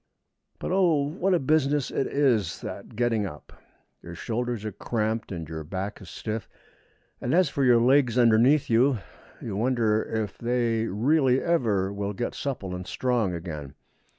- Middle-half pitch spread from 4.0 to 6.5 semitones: Yes, average, 4.7 semitones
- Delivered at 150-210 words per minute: Yes, average, 160 wpm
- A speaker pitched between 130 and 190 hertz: No, low, 115 Hz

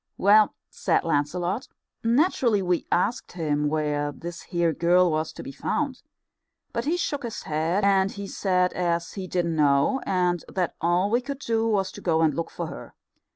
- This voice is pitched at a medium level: Yes, medium, 180 Hz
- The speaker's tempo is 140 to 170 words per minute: No, average, 180 wpm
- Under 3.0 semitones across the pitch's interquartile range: No, average, 4.3 semitones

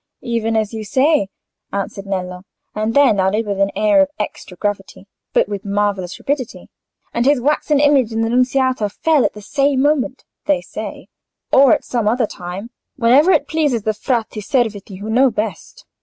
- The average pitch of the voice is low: No, high, 225 Hz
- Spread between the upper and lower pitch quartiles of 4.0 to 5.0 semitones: Yes, average, 4.7 semitones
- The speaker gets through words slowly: No, average, 175 wpm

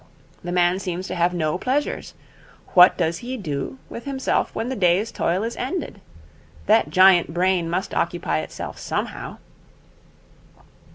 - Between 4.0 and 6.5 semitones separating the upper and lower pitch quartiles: Yes, average, 4.6 semitones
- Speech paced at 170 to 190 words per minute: No, average, 145 wpm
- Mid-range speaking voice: Yes, medium, 180 Hz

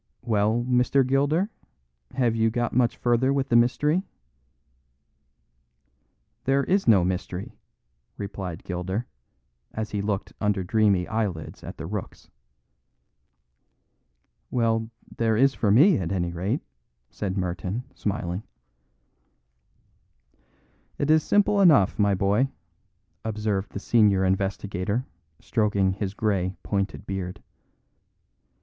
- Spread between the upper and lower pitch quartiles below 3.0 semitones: No, average, 4.2 semitones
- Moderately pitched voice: No, low, 105 Hz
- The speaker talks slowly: Yes, slow, 110 wpm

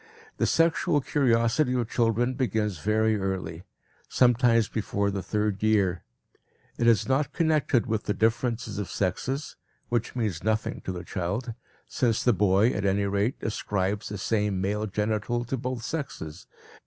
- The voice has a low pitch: Yes, low, 110 Hz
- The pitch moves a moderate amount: Yes, average, 3.3 semitones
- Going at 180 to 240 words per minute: No, average, 150 wpm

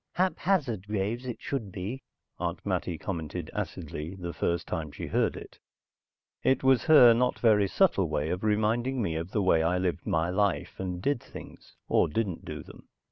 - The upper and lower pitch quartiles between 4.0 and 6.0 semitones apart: Yes, wide, 5.4 semitones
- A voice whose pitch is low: Yes, very low, 95 Hz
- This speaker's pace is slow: No, average, 180 wpm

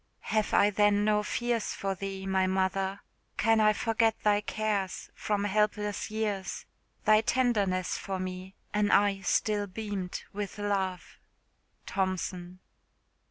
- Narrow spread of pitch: Yes, narrow, 1.9 semitones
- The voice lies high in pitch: Yes, high, 205 Hz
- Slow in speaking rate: Yes, slow, 125 wpm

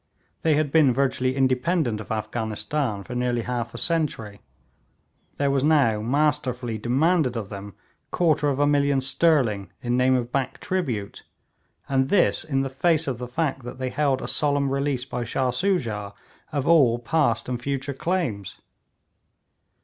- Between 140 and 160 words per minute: Yes, average, 155 wpm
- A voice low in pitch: Yes, low, 130 Hz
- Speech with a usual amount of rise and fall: Yes, average, 3.6 semitones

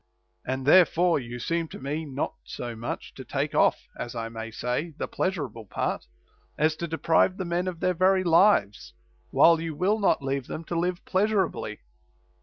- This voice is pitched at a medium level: Yes, medium, 165 Hz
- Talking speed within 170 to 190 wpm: Yes, average, 180 wpm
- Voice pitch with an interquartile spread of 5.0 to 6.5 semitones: Yes, wide, 5.6 semitones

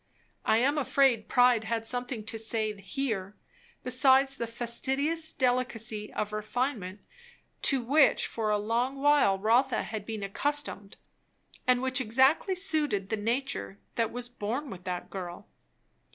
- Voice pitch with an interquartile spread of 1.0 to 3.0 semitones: No, average, 4.0 semitones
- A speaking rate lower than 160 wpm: Yes, slow, 135 wpm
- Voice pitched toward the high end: Yes, high, 235 Hz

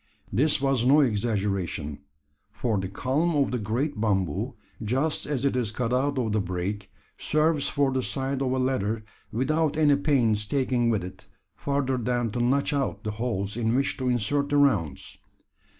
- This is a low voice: Yes, low, 125 Hz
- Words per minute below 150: No, average, 175 wpm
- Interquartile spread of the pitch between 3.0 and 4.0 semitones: No, average, 4.8 semitones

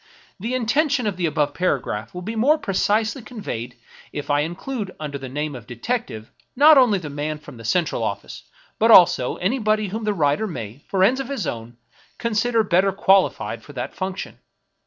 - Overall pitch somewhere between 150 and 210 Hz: Yes, high, 190 Hz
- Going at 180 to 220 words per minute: Yes, average, 190 wpm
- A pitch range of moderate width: No, wide, 7.5 semitones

